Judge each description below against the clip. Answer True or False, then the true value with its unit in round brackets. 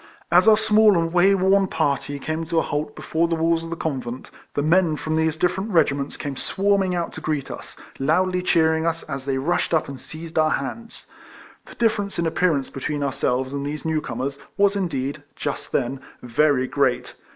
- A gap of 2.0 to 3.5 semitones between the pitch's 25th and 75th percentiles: False (4.2 semitones)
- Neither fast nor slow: True (195 wpm)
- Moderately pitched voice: True (160 Hz)